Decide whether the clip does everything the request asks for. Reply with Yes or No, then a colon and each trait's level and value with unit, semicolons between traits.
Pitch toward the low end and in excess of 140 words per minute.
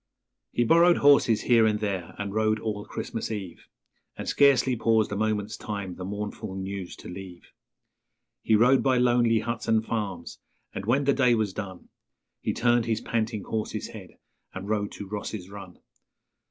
Yes: low, 110 Hz; average, 170 wpm